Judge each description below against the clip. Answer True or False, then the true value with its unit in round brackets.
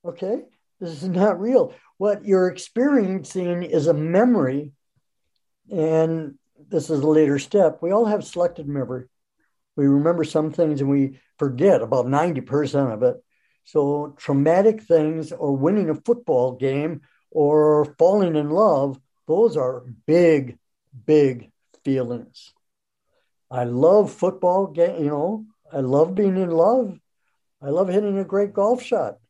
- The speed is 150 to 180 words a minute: False (140 wpm)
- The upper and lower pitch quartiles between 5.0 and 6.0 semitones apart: True (5.3 semitones)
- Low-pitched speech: False (160 Hz)